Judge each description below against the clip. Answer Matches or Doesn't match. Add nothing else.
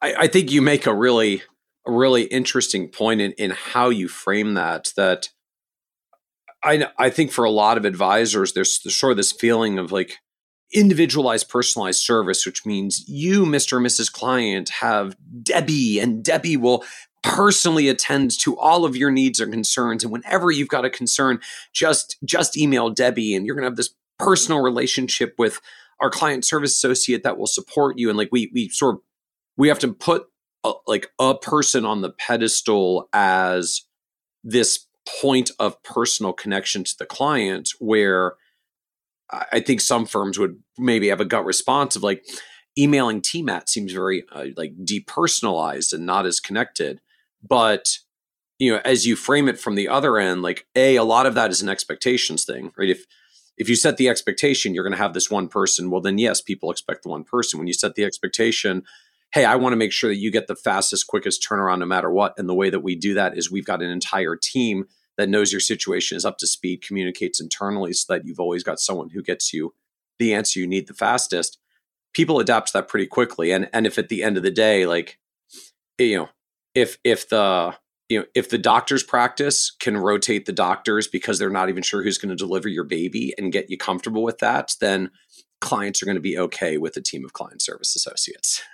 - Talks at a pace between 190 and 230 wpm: Matches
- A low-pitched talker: Matches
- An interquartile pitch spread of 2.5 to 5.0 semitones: Doesn't match